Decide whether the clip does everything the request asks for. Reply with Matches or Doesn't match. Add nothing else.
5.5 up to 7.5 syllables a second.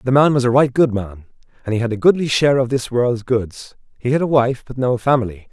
Matches